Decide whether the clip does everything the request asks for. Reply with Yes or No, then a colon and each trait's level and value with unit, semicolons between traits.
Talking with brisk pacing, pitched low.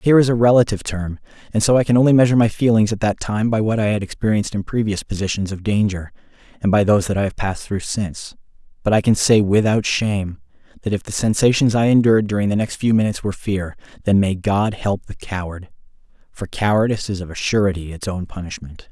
Yes: fast, 220 wpm; low, 105 Hz